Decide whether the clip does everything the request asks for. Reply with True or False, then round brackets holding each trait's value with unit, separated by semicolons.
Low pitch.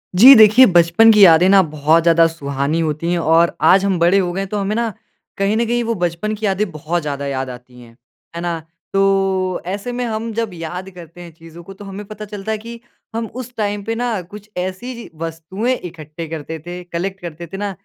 False (185 Hz)